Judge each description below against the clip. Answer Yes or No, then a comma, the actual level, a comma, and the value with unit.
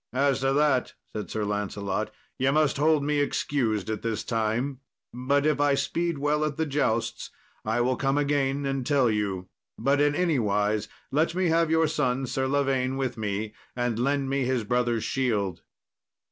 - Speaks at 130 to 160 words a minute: No, average, 175 wpm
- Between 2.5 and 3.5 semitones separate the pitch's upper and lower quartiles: No, average, 4.3 semitones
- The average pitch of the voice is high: No, low, 135 Hz